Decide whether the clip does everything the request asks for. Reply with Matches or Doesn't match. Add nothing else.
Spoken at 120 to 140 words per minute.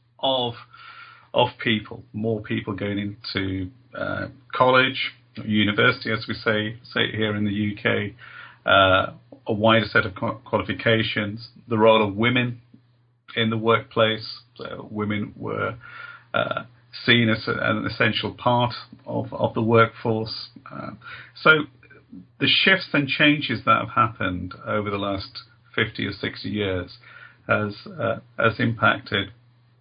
Matches